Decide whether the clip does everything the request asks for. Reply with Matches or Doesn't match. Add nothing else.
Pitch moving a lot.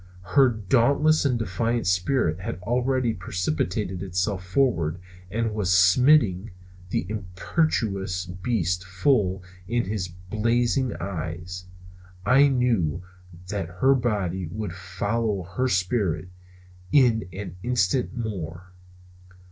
Doesn't match